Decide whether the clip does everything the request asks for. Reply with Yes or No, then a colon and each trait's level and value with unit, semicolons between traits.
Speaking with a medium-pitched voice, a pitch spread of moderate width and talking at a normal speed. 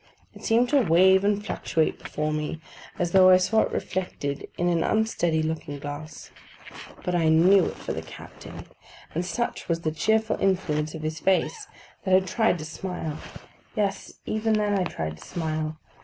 Yes: medium, 175 Hz; average, 4.3 semitones; average, 175 wpm